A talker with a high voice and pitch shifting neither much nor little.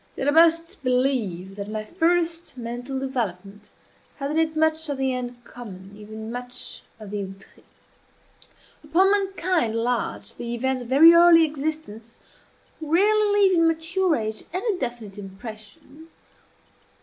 No: very high, 265 Hz; wide, 7.0 semitones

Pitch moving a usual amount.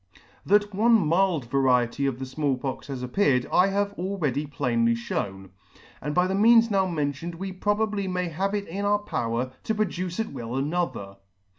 No: wide, 7.2 semitones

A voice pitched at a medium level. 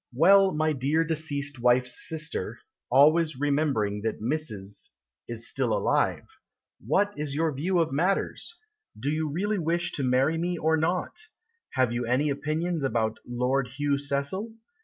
Yes: medium, 145 Hz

